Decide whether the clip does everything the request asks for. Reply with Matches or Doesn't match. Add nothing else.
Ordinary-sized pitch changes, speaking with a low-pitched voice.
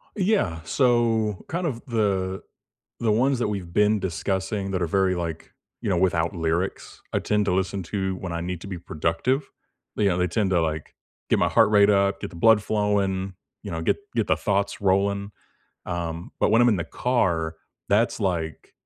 Matches